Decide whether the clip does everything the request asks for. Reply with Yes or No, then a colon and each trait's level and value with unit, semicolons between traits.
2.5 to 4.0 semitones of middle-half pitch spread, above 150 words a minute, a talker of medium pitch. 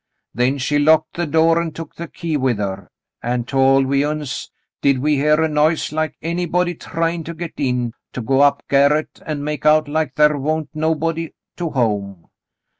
Yes: average, 3.0 semitones; average, 185 wpm; medium, 150 Hz